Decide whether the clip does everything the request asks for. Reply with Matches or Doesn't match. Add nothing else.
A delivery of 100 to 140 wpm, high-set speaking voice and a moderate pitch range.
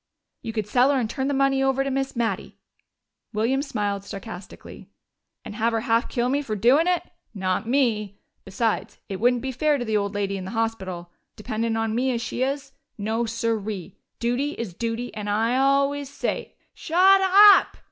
Doesn't match